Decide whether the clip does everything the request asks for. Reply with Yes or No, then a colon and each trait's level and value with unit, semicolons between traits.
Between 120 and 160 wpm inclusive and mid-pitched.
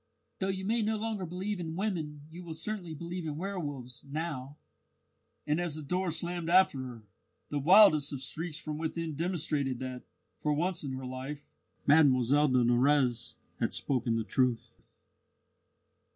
Yes: average, 155 wpm; medium, 155 Hz